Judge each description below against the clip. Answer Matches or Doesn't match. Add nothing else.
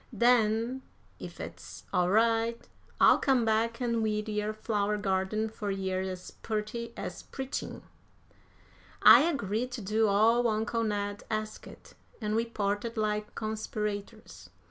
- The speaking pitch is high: Matches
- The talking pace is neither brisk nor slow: Doesn't match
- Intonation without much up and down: Matches